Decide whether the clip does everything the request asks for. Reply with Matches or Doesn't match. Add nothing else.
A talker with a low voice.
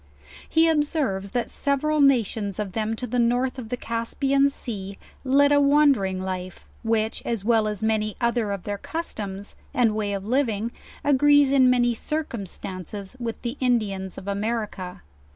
Doesn't match